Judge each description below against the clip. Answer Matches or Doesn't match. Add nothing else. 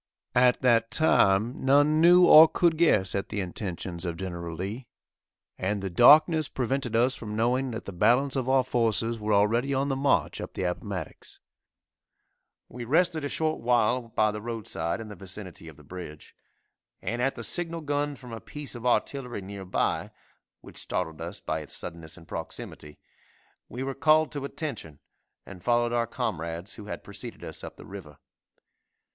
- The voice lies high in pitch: Doesn't match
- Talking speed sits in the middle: Matches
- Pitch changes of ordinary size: Doesn't match